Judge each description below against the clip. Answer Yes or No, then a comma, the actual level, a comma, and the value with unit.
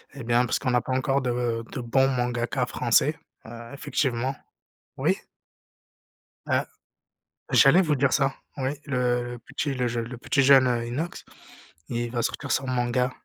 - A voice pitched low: Yes, low, 125 Hz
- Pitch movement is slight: Yes, narrow, 2.2 semitones